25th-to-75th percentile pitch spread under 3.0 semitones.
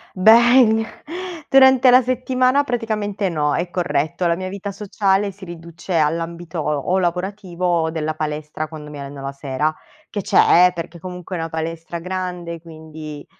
No: average, 4.0 semitones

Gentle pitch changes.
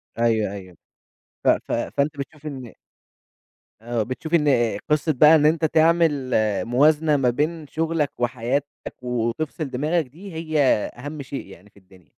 No: average, 4.5 semitones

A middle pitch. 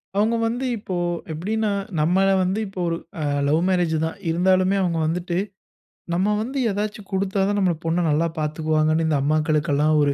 Yes: medium, 175 Hz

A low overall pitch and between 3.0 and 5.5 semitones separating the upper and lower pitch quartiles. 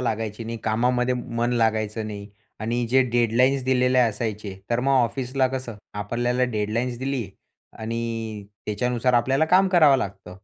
No: low, 120 Hz; narrow, 2.5 semitones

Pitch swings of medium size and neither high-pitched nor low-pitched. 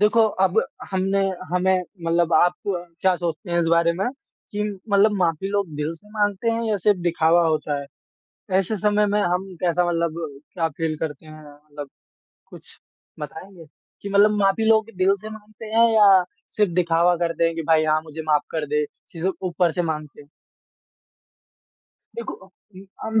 Yes: average, 3.7 semitones; medium, 175 Hz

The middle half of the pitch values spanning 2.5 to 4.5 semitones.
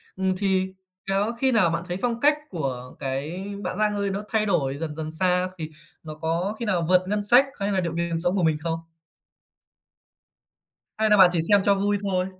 Yes: average, 3.7 semitones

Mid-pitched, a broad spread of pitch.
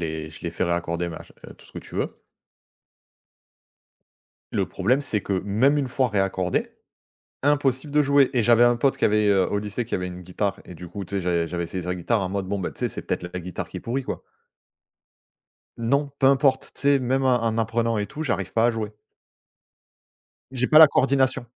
No: low, 110 Hz; wide, 6.3 semitones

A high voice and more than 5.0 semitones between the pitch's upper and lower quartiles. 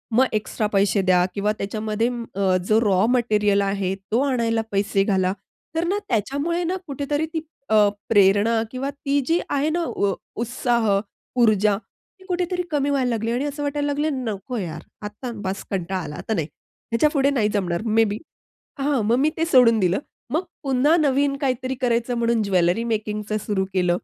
Yes: high, 230 Hz; wide, 5.6 semitones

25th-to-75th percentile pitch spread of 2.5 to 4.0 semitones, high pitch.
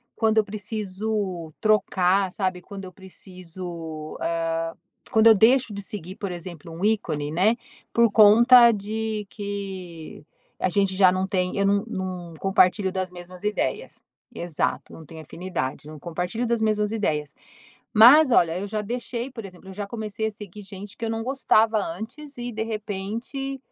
Yes: average, 3.5 semitones; high, 200 Hz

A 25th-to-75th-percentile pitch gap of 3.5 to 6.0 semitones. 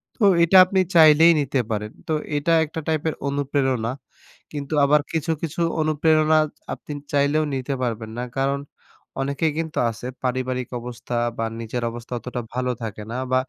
Yes: average, 4.0 semitones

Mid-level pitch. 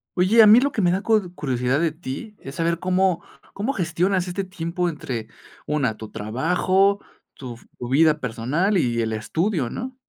Yes: medium, 170 Hz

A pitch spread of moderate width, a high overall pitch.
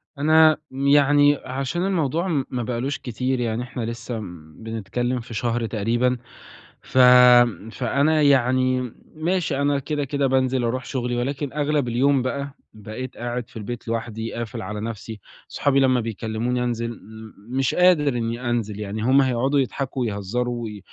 No: average, 3.2 semitones; low, 125 Hz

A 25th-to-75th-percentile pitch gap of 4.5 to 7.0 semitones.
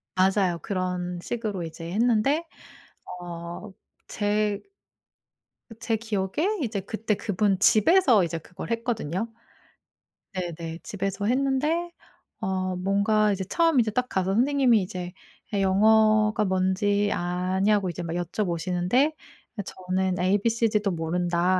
No: average, 3.3 semitones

